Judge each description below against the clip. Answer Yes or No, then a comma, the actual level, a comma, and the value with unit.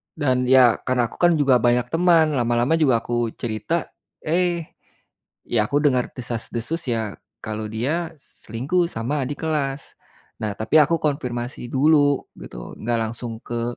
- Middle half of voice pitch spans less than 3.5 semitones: No, average, 4.7 semitones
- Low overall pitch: Yes, low, 130 Hz